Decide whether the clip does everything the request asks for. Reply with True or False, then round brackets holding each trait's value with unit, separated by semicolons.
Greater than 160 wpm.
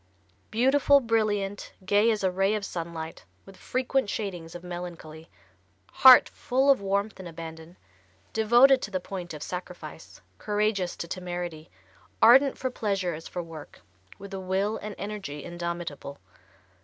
False (145 wpm)